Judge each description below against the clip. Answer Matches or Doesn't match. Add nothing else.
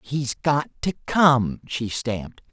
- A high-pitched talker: Doesn't match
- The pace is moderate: Matches